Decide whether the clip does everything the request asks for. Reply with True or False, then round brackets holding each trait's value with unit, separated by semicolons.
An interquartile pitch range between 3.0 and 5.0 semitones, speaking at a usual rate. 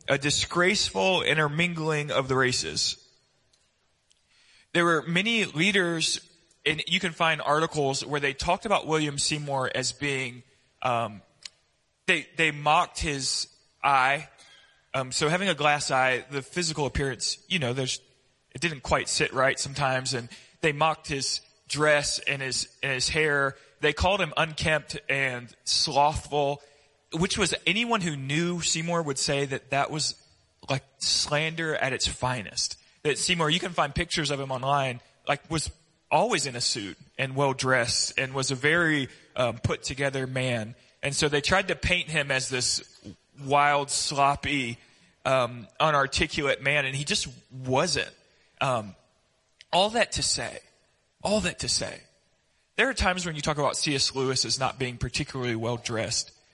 True (3.4 semitones; 155 wpm)